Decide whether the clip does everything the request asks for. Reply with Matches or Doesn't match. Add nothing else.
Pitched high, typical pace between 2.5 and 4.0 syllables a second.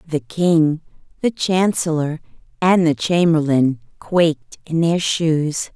Doesn't match